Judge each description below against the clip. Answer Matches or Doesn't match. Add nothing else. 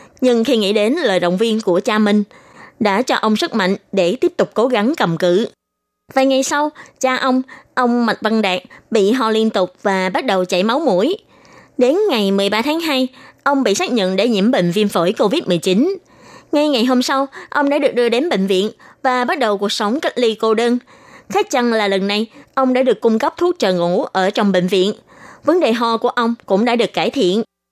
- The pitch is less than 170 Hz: Doesn't match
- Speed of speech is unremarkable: Matches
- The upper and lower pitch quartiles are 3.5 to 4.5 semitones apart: Doesn't match